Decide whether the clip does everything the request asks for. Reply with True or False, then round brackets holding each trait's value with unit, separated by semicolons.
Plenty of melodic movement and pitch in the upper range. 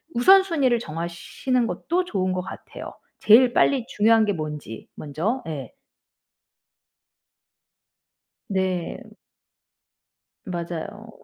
True (6.4 semitones; 205 Hz)